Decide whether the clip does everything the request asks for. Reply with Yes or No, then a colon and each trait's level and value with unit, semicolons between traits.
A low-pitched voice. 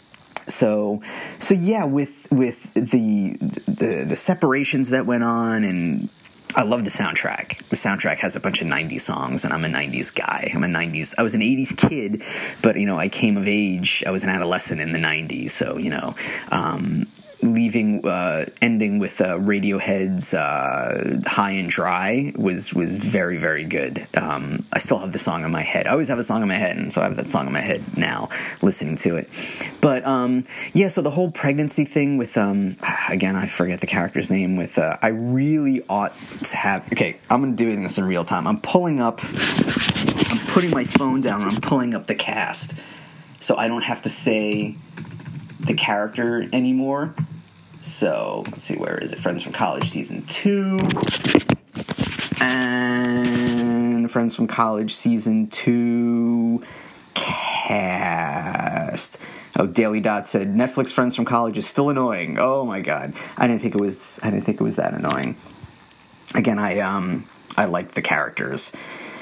Yes: low, 120 Hz